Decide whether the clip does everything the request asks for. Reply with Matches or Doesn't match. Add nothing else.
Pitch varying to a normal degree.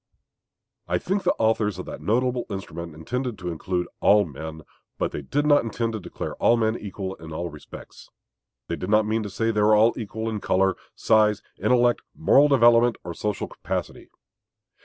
Matches